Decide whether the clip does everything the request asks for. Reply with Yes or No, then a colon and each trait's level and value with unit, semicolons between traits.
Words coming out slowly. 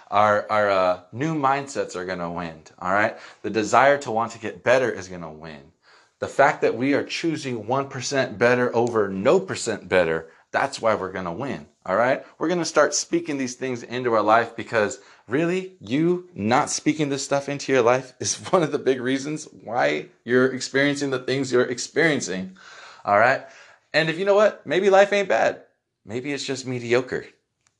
No: average, 185 wpm